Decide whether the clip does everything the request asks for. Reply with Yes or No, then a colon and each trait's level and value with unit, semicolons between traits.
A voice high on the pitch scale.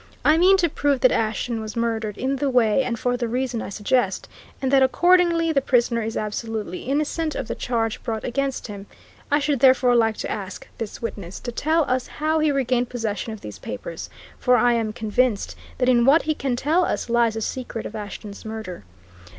Yes: high, 245 Hz